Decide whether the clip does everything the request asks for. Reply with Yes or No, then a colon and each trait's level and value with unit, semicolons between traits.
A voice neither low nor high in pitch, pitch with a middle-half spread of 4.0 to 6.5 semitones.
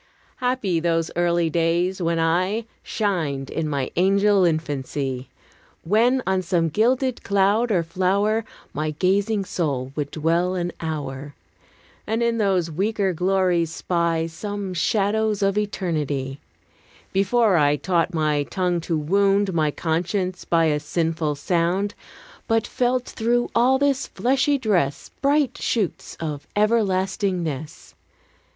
Yes: medium, 180 Hz; average, 4.3 semitones